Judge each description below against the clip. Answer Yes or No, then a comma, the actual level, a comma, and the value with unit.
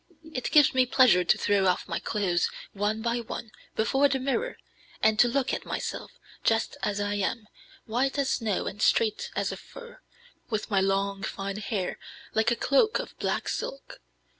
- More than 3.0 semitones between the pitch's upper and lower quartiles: Yes, average, 4.5 semitones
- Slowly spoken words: No, average, 180 wpm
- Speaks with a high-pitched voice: Yes, high, 220 Hz